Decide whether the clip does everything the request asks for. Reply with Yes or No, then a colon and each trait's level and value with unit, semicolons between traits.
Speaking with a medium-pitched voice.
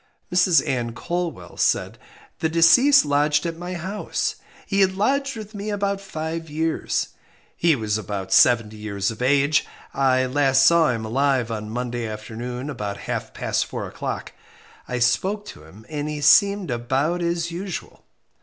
Yes: medium, 145 Hz